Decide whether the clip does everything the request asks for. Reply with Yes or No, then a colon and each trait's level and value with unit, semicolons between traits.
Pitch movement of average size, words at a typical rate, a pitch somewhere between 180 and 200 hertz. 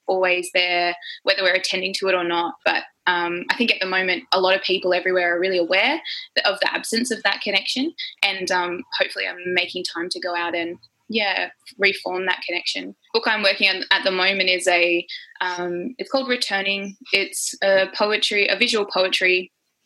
No: narrow, 2.0 semitones; average, 195 wpm; medium, 185 Hz